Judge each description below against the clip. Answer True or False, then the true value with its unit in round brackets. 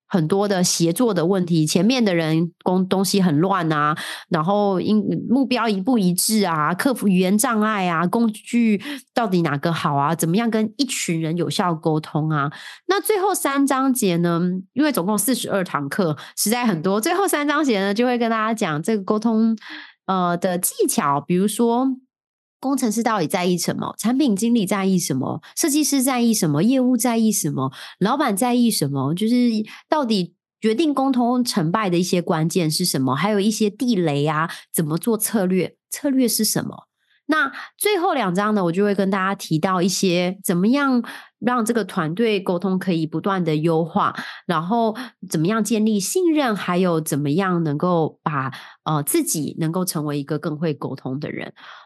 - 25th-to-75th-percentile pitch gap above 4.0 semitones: True (5.3 semitones)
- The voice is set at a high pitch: True (200 Hz)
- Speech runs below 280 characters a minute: True (270 characters per minute)